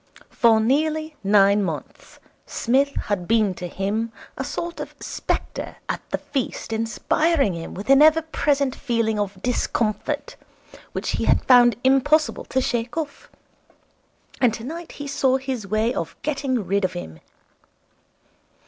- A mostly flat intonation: No, average, 5.2 semitones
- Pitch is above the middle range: Yes, high, 240 Hz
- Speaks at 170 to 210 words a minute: No, average, 140 wpm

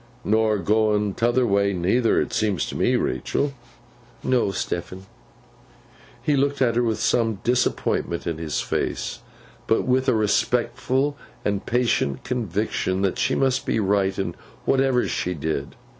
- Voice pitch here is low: Yes, low, 110 Hz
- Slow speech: No, average, 145 wpm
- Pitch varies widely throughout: No, average, 4.4 semitones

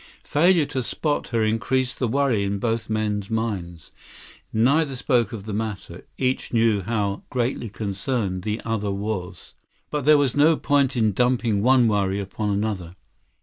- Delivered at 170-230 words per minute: No, average, 155 wpm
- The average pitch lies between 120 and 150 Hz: No, low, 110 Hz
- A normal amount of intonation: Yes, average, 4.2 semitones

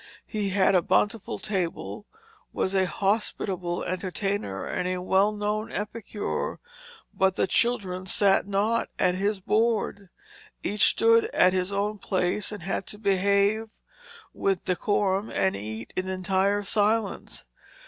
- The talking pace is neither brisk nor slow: No, slow, 125 wpm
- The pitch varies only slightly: Yes, narrow, 2.1 semitones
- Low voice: No, high, 195 Hz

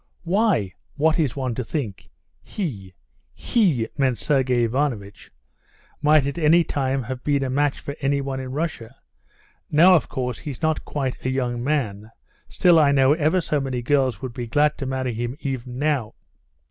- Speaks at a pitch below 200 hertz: Yes, low, 135 Hz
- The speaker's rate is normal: Yes, average, 170 wpm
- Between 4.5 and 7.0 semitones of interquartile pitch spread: No, average, 3.4 semitones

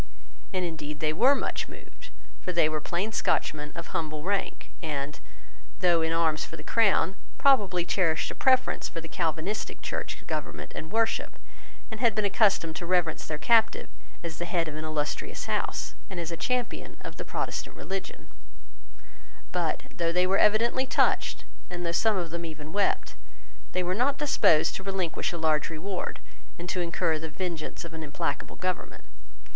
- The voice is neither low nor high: Yes, medium, 175 Hz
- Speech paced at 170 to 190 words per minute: Yes, average, 175 wpm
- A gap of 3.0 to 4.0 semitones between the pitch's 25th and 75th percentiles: Yes, average, 3.6 semitones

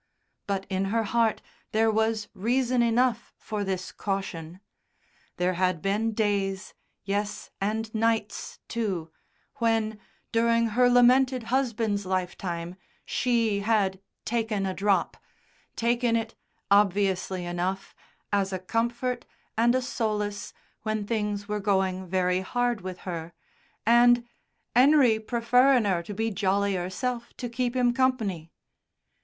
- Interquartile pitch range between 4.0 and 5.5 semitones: No, average, 3.5 semitones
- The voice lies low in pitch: No, high, 215 Hz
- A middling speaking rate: No, slow, 125 wpm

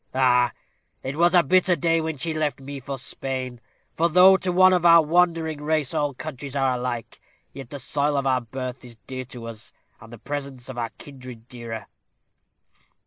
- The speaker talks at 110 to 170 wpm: No, average, 190 wpm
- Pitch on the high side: No, low, 135 Hz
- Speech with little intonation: No, average, 4.1 semitones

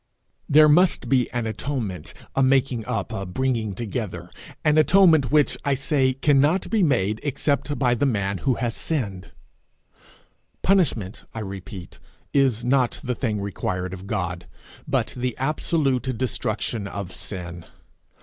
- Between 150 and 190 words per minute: No, average, 140 wpm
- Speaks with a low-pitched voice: Yes, low, 125 Hz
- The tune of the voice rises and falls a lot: Yes, wide, 5.7 semitones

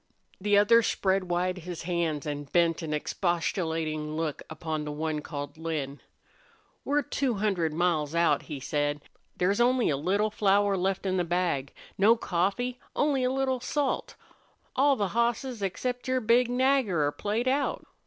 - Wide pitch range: Yes, wide, 6.7 semitones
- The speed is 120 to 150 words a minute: No, average, 160 wpm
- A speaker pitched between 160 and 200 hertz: Yes, medium, 185 Hz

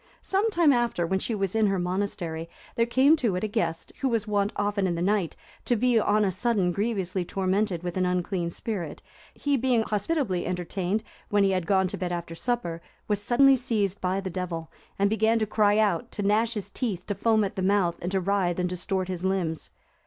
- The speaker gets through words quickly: Yes, fast, 215 wpm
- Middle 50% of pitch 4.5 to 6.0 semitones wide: No, average, 3.5 semitones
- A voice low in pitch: No, high, 200 Hz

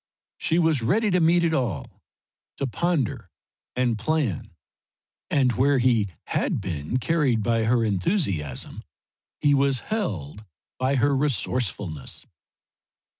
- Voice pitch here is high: No, low, 130 Hz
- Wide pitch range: Yes, wide, 6.3 semitones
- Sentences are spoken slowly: Yes, slow, 120 wpm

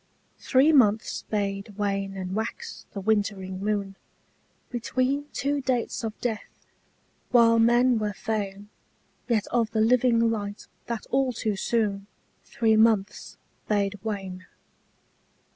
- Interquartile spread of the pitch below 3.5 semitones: Yes, average, 3.0 semitones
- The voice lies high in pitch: Yes, high, 220 Hz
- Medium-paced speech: No, slow, 120 wpm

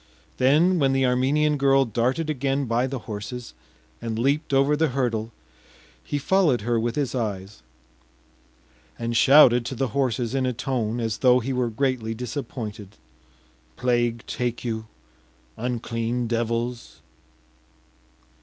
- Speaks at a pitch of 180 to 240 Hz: No, low, 125 Hz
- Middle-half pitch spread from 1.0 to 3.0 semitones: Yes, average, 2.7 semitones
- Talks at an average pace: No, slow, 130 wpm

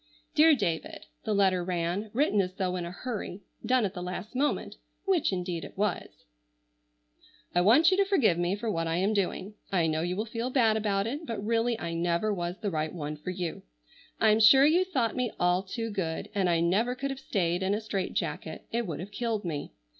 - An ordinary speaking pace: No, fast, 210 wpm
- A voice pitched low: No, high, 200 Hz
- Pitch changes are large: No, average, 4.6 semitones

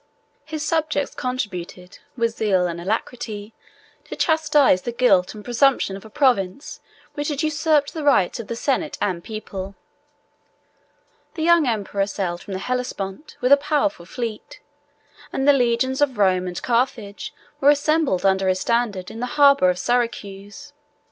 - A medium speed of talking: Yes, average, 155 wpm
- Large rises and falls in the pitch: Yes, wide, 6.6 semitones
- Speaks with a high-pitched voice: Yes, high, 235 Hz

